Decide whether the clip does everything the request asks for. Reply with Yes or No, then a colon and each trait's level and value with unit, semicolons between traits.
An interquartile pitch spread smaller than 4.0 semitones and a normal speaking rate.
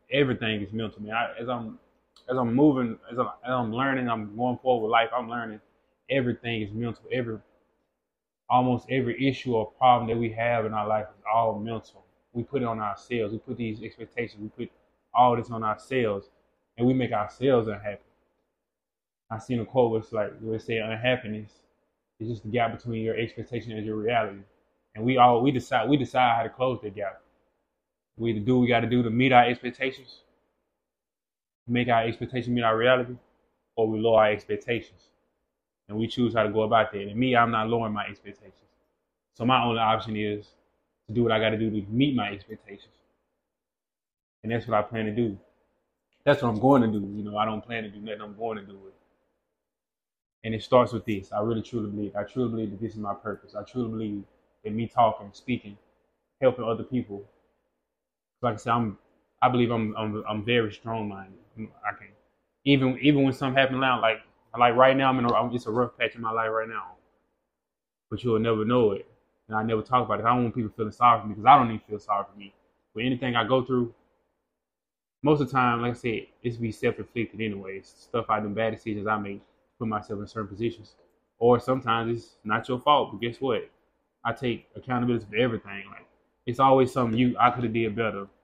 No: narrow, 2.4 semitones; fast, 210 wpm